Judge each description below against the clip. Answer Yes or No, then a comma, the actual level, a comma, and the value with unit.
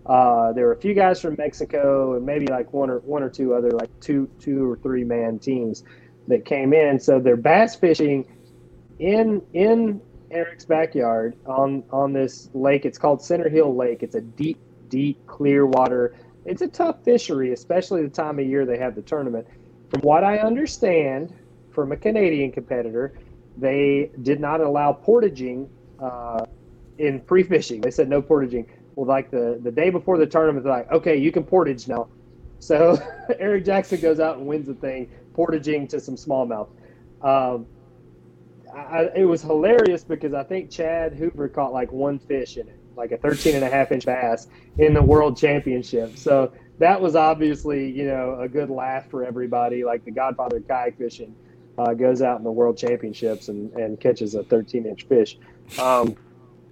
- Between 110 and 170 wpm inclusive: No, average, 180 wpm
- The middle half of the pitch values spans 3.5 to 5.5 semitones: Yes, average, 4.2 semitones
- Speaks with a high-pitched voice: No, medium, 140 Hz